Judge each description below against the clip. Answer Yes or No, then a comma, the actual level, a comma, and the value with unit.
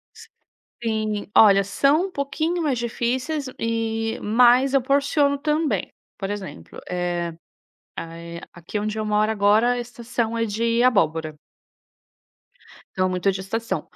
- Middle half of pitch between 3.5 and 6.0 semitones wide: Yes, average, 4.3 semitones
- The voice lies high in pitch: Yes, high, 225 Hz